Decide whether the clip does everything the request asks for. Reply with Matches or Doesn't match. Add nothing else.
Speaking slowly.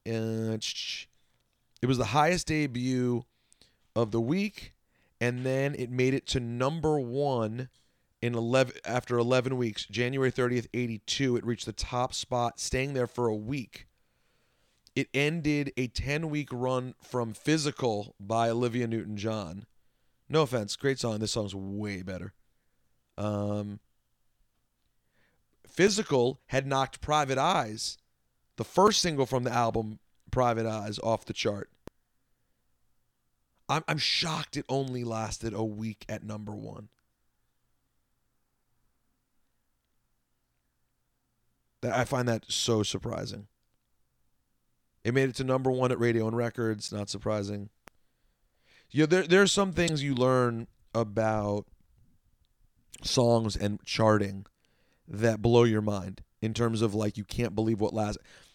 Matches